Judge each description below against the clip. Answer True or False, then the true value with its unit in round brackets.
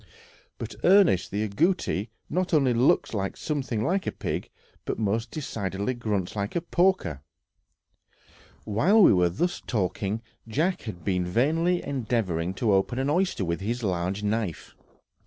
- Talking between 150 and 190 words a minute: False (140 wpm)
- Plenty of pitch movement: True (7.9 semitones)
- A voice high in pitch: False (115 Hz)